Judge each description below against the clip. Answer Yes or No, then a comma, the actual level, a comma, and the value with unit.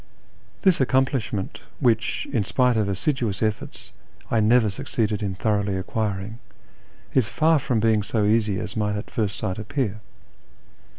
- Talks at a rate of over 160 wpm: No, average, 140 wpm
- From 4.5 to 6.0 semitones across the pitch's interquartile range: No, average, 3.1 semitones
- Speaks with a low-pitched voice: Yes, low, 110 Hz